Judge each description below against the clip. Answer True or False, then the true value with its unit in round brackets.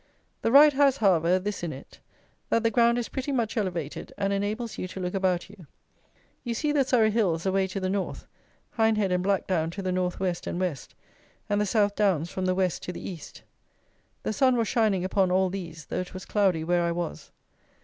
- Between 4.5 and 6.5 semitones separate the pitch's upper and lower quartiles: False (3.5 semitones)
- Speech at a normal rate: False (210 wpm)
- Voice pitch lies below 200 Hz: True (190 Hz)